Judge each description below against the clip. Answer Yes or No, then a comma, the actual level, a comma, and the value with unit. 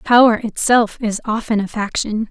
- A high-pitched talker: Yes, high, 220 Hz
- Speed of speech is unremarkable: Yes, average, 155 wpm